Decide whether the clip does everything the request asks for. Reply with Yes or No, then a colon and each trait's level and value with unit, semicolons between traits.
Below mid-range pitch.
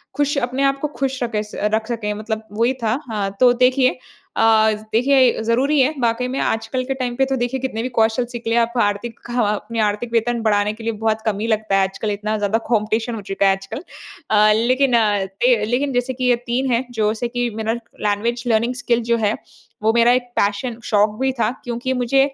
No: high, 230 Hz